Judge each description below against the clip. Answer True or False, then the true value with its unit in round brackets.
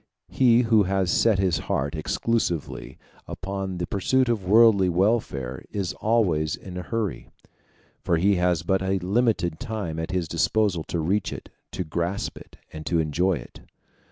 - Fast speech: False (160 wpm)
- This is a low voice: True (95 Hz)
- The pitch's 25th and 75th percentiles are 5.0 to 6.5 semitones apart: False (4.0 semitones)